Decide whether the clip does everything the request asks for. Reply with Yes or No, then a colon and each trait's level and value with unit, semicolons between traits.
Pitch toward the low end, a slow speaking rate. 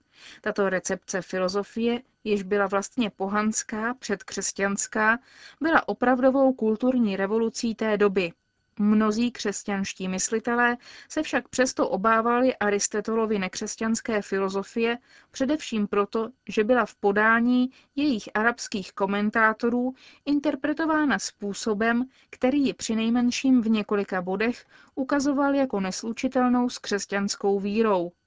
No: high, 225 Hz; slow, 100 wpm